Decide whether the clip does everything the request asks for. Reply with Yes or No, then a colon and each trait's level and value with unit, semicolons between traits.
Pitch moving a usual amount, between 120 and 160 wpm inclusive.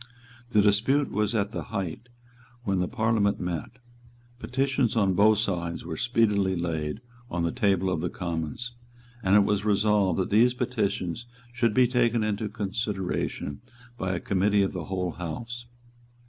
Yes: average, 3.9 semitones; average, 155 wpm